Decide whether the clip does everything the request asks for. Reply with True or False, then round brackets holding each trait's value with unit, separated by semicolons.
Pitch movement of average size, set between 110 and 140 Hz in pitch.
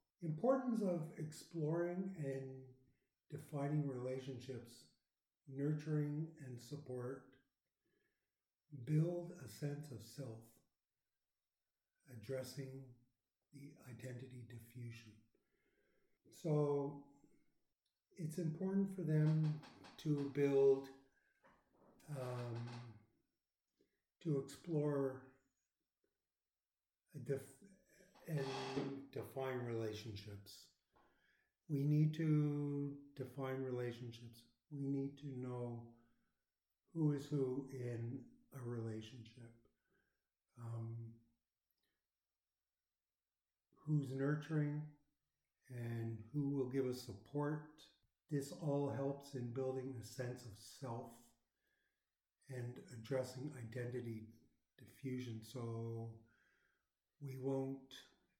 True (3.5 semitones; 135 Hz)